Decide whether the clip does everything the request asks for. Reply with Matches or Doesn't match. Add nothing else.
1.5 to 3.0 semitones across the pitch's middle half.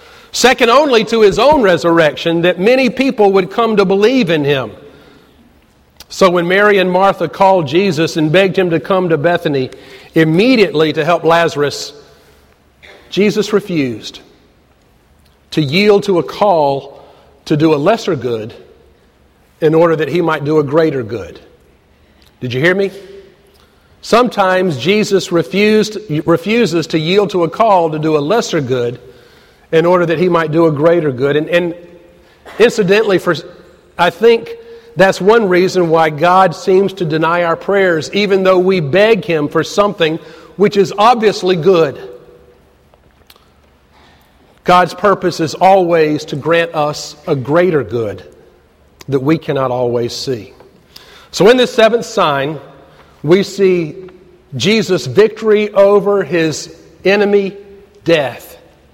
Doesn't match